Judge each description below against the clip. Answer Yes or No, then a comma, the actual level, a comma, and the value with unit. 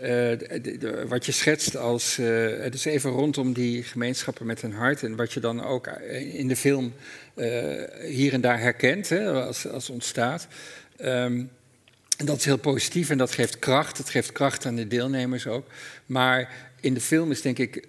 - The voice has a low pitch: Yes, low, 130 Hz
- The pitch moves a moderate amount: No, narrow, 2.1 semitones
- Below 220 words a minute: Yes, average, 195 wpm